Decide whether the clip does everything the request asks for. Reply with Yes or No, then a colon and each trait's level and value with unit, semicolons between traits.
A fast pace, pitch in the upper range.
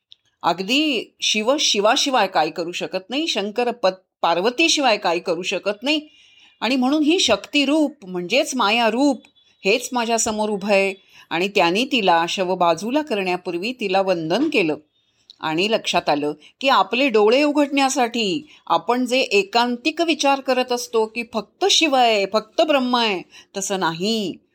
Yes: fast, 140 wpm; high, 225 Hz